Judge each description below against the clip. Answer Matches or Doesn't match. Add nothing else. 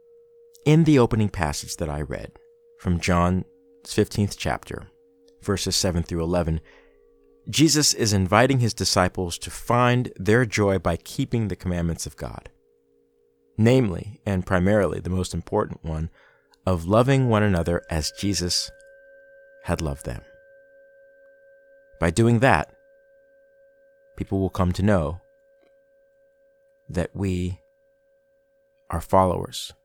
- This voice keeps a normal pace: Doesn't match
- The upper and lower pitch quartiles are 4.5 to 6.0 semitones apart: Matches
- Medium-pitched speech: Doesn't match